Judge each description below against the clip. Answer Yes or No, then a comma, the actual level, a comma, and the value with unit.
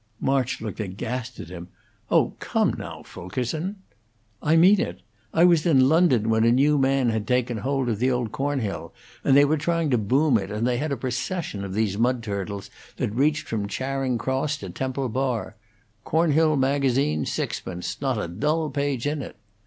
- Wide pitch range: No, average, 4.6 semitones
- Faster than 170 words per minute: Yes, average, 180 wpm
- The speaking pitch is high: No, low, 130 Hz